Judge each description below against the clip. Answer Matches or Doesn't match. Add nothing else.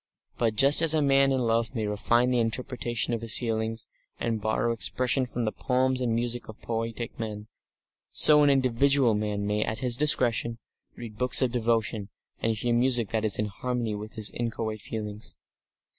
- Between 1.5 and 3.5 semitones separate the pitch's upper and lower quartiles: Matches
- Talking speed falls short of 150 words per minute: Doesn't match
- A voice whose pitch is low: Matches